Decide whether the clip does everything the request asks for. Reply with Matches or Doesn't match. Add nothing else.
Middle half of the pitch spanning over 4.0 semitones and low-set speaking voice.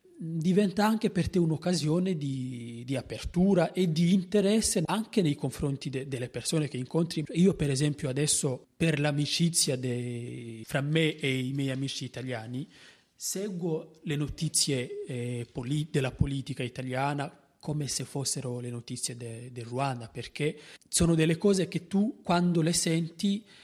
Doesn't match